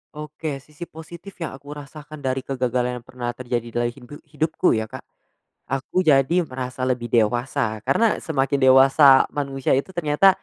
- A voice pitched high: No, low, 135 Hz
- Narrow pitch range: No, average, 3.2 semitones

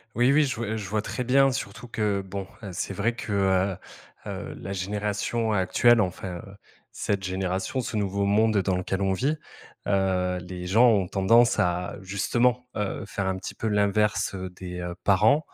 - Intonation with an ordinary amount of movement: Yes, average, 3.0 semitones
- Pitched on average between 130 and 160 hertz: No, low, 100 Hz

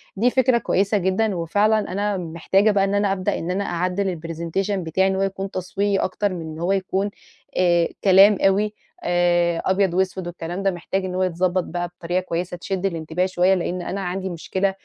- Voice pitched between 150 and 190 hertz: Yes, medium, 185 Hz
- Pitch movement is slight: Yes, narrow, 2.0 semitones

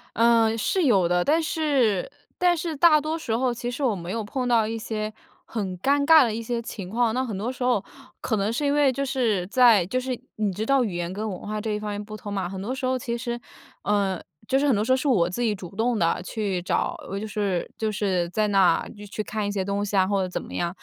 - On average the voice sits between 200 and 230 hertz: Yes, high, 220 Hz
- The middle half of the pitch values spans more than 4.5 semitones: No, average, 4.2 semitones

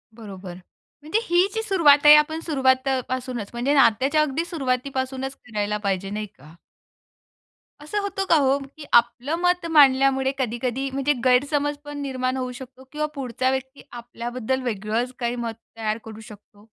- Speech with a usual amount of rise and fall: Yes, average, 3.4 semitones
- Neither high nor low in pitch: No, very high, 260 Hz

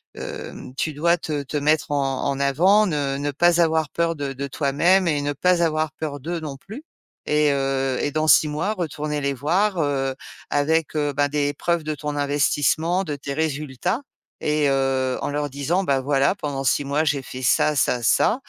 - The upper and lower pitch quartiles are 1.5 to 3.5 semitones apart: Yes, narrow, 2.5 semitones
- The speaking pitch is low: No, medium, 145 Hz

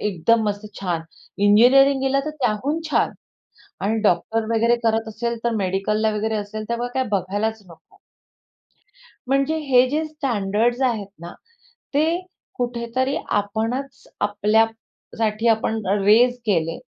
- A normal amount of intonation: Yes, average, 3.2 semitones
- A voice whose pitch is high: Yes, high, 225 Hz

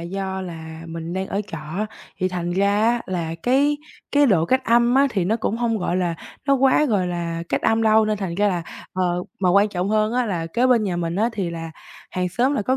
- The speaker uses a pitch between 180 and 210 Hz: Yes, high, 195 Hz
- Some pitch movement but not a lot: Yes, average, 4.7 semitones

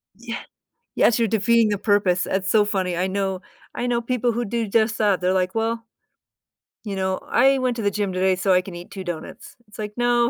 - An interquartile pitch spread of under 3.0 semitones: No, average, 3.6 semitones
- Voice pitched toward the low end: No, high, 205 Hz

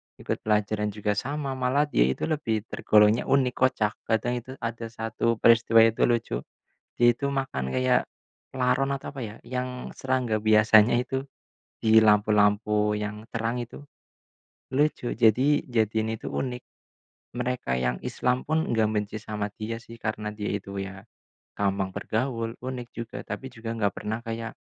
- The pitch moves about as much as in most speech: Yes, average, 3.0 semitones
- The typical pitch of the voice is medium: No, low, 115 Hz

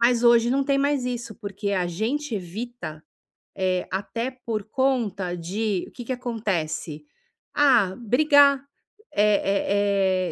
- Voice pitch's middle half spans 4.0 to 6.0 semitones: Yes, average, 4.7 semitones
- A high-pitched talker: Yes, high, 220 Hz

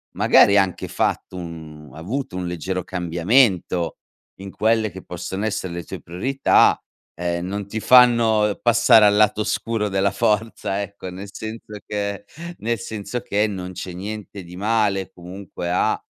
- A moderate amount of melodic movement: Yes, average, 3.2 semitones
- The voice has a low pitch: Yes, low, 100 Hz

